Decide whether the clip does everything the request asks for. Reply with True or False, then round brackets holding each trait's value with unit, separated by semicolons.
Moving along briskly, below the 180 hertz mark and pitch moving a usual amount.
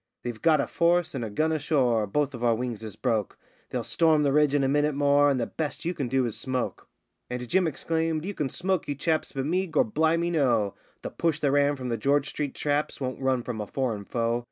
True (245 wpm; 140 Hz; 4.3 semitones)